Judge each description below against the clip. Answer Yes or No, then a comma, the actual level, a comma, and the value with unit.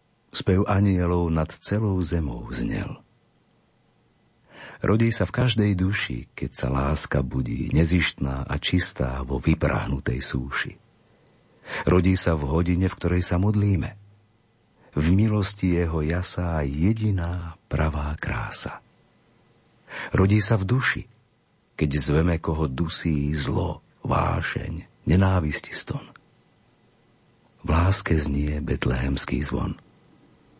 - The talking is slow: Yes, slow, 105 wpm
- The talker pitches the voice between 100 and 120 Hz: No, very low, 85 Hz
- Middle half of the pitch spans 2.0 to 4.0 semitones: No, average, 4.9 semitones